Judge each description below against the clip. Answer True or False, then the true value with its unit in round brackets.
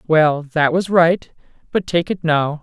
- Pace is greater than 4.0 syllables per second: False (3.8 syllables/s)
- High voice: False (165 Hz)